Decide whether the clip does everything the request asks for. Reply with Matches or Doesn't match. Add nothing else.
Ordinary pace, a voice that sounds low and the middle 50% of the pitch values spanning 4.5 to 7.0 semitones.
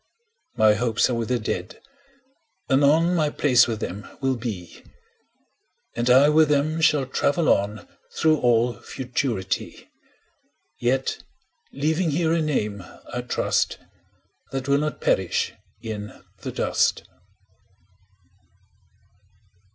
Doesn't match